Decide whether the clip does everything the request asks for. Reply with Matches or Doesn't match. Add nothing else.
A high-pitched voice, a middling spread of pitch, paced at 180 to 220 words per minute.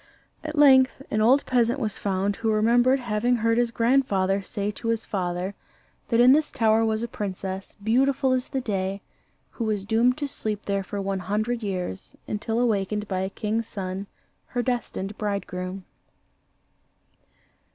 Doesn't match